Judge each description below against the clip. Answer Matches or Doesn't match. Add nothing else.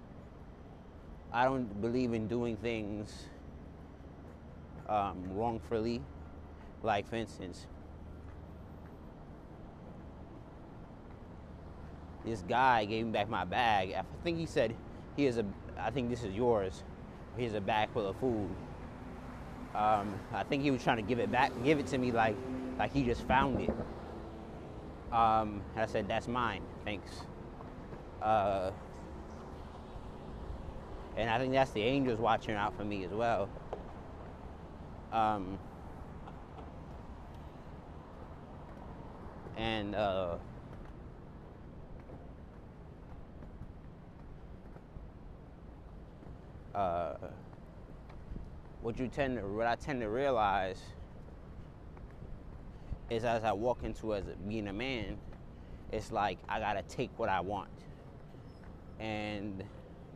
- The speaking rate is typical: Doesn't match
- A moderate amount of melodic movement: Doesn't match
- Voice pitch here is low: Matches